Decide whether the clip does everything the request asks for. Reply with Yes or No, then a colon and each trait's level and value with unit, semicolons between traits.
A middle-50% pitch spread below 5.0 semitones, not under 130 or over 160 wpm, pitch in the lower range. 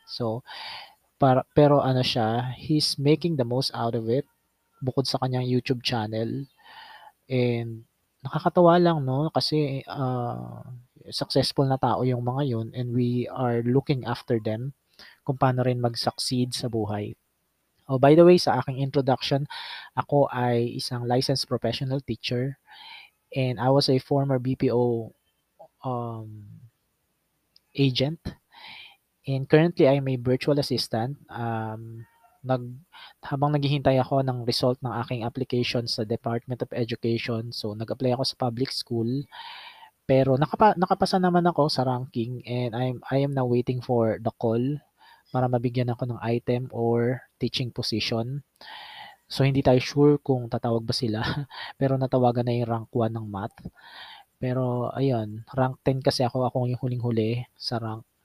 Yes: average, 2.7 semitones; average, 140 wpm; low, 125 Hz